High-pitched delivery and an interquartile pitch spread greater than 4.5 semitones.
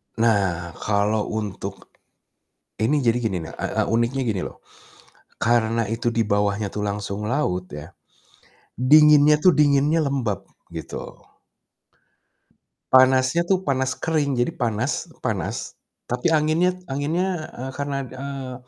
No: low, 125 Hz; average, 5.3 semitones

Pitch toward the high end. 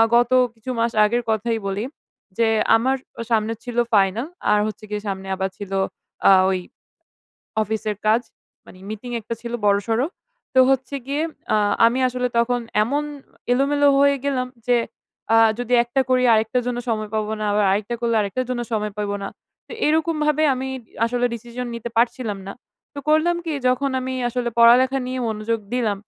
Yes: high, 235 Hz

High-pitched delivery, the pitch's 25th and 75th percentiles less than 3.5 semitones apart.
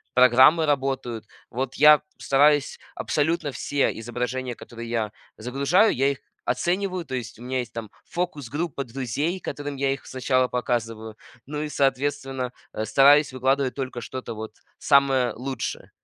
No: low, 135 Hz; average, 2.8 semitones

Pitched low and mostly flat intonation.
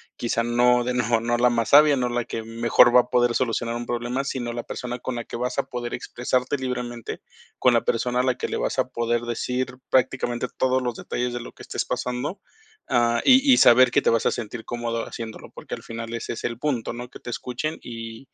Yes: low, 120 Hz; narrow, 1.1 semitones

